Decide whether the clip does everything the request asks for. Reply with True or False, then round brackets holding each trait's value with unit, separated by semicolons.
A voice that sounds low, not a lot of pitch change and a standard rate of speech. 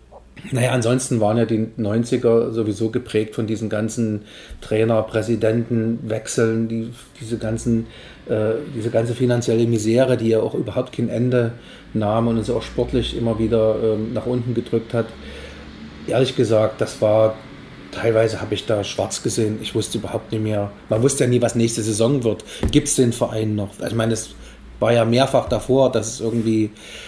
True (115 Hz; 1.4 semitones; 170 wpm)